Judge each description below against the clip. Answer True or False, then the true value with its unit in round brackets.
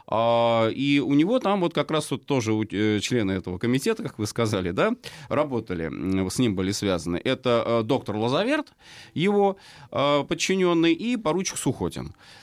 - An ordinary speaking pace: True (140 wpm)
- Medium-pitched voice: False (125 Hz)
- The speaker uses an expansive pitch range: True (7.0 semitones)